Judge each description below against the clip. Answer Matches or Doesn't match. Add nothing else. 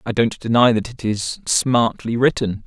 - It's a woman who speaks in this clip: Doesn't match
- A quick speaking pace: Doesn't match